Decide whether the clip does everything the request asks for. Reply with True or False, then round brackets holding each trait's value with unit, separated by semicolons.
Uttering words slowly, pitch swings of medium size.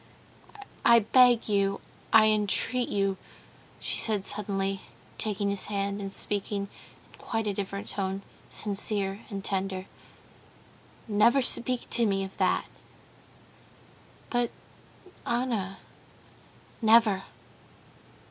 False (100 wpm; 2.3 semitones)